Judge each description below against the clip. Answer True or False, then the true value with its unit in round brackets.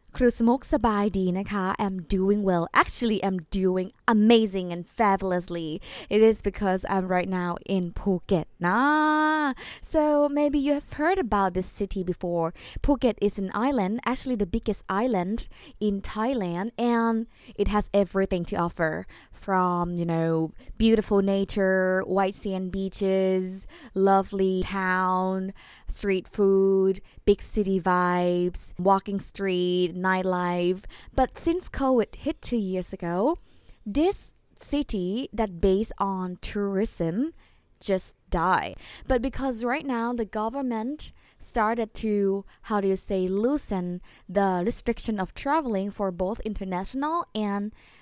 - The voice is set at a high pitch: True (200 Hz)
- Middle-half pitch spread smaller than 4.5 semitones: True (3.9 semitones)